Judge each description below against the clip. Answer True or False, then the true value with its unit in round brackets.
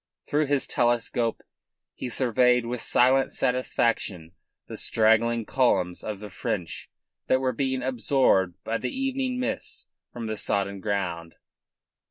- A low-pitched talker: True (120 Hz)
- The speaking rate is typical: False (130 wpm)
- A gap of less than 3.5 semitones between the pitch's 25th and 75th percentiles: False (3.9 semitones)